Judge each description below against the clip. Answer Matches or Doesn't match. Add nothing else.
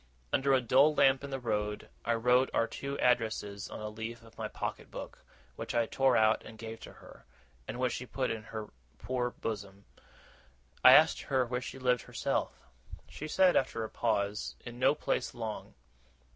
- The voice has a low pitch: Matches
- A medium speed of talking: Matches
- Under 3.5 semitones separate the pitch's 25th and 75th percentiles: Matches